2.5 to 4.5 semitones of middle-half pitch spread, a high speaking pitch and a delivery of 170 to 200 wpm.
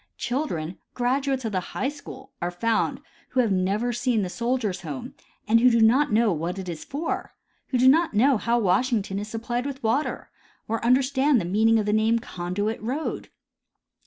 Yes: average, 4.2 semitones; high, 230 Hz; average, 180 wpm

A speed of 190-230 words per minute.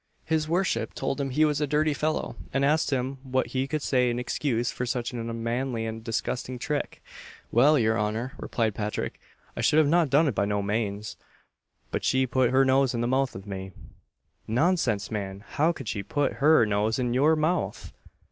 Yes: average, 195 wpm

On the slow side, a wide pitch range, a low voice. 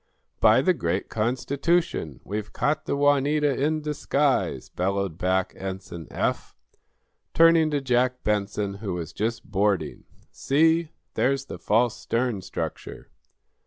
Yes: slow, 125 wpm; wide, 6.6 semitones; low, 120 Hz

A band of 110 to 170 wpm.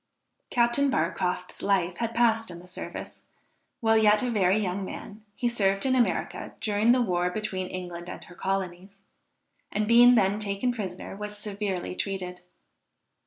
Yes: average, 155 wpm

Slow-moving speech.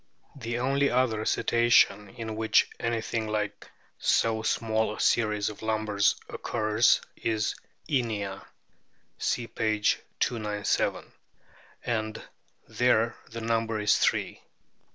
Yes: slow, 105 wpm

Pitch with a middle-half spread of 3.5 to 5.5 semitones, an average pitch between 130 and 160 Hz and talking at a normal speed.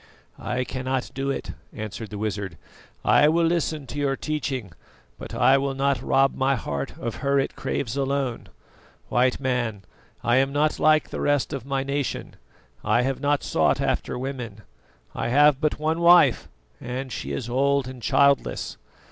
No: narrow, 2.4 semitones; low, 135 Hz; average, 165 wpm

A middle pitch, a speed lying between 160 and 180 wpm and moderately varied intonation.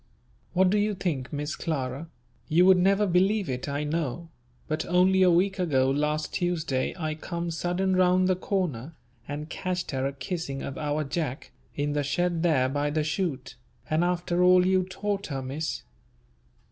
Yes: medium, 165 Hz; average, 170 wpm; average, 4.0 semitones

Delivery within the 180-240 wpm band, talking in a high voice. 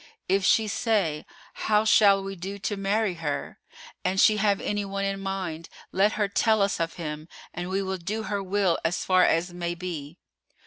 Yes: average, 190 wpm; high, 195 Hz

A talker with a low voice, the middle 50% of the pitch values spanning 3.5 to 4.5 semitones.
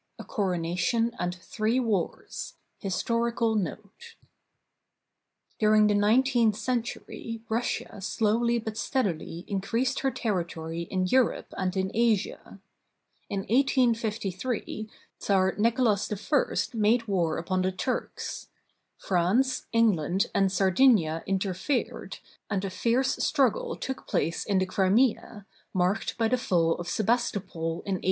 No: high, 210 Hz; average, 4.0 semitones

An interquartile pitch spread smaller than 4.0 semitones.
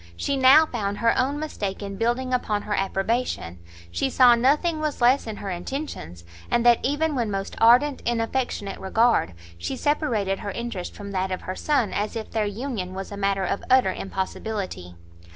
No: average, 4.8 semitones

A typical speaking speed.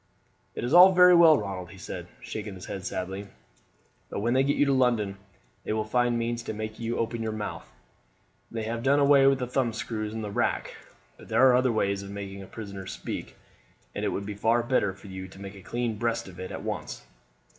No: fast, 225 wpm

